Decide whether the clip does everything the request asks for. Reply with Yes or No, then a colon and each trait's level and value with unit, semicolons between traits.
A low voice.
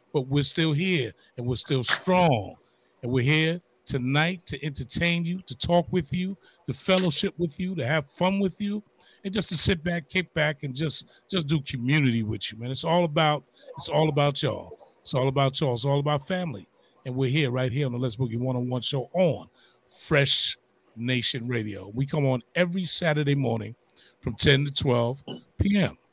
No: medium, 145 Hz